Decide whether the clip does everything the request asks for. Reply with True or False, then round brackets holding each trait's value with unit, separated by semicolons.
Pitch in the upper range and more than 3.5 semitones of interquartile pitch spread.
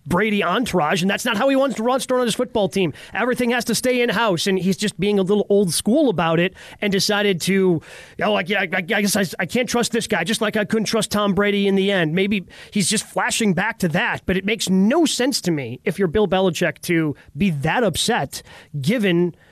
False (200 Hz; 3.1 semitones)